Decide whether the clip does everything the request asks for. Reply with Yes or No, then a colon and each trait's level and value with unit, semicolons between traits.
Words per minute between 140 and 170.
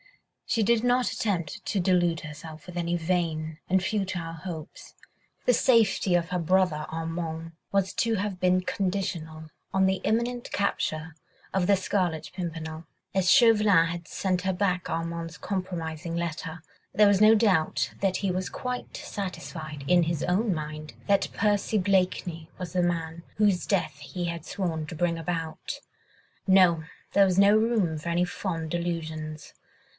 Yes: average, 155 wpm